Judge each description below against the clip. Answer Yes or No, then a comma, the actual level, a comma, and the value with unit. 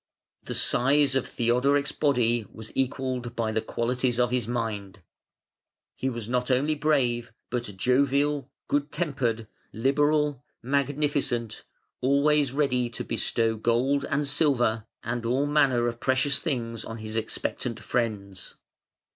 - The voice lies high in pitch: No, low, 125 Hz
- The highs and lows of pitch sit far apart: No, average, 3.3 semitones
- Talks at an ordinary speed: No, slow, 130 wpm